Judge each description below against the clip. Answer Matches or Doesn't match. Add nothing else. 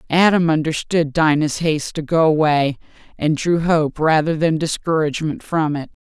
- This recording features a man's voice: Doesn't match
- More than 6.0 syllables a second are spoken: Doesn't match